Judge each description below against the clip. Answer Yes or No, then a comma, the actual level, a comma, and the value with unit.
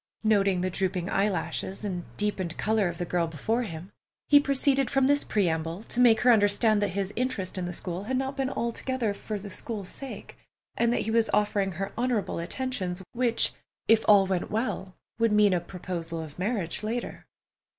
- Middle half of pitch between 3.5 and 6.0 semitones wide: Yes, average, 4.3 semitones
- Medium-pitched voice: No, high, 205 Hz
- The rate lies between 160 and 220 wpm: Yes, average, 185 wpm